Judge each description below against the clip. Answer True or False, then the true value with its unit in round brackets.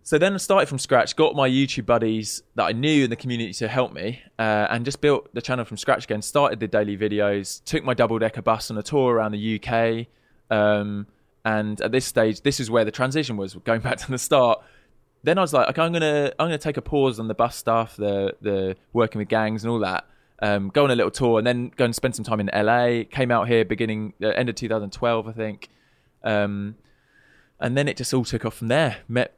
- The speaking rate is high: True (245 wpm)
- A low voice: True (115 Hz)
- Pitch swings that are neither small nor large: True (3.1 semitones)